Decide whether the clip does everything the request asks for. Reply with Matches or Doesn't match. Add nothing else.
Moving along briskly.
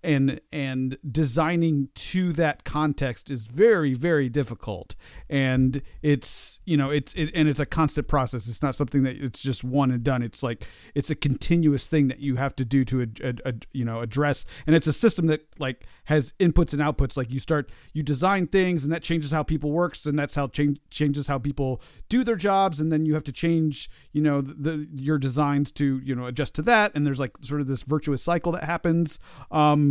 Matches